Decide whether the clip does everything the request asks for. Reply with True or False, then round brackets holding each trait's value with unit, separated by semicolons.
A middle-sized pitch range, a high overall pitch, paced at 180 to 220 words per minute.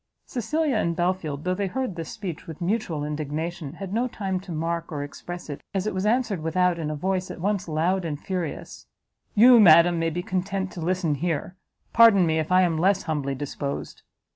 False (3.3 semitones; 175 Hz; 200 wpm)